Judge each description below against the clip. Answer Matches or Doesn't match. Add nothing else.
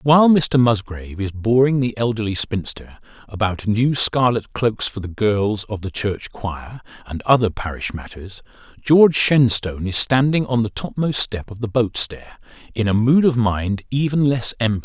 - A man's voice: Matches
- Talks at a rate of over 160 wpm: Matches